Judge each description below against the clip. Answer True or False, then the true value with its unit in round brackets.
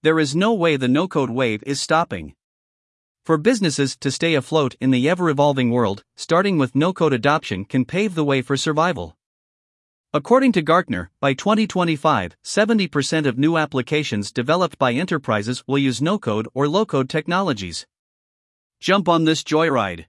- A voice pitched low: False (150 Hz)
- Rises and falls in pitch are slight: False (4.5 semitones)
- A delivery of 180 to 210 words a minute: False (165 wpm)